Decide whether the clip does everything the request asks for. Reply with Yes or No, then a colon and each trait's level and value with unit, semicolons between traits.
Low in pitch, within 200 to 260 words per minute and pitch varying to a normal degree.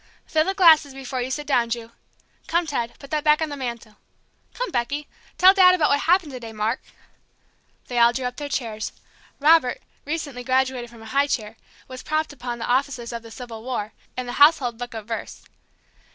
No: very high, 260 Hz; fast, 205 wpm; average, 4.0 semitones